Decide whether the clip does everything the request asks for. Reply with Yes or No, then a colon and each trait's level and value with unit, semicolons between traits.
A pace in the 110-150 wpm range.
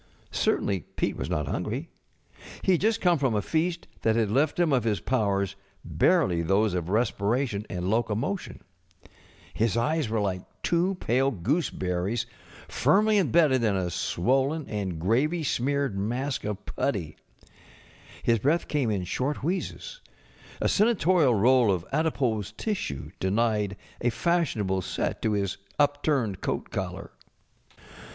Yes: average, 140 wpm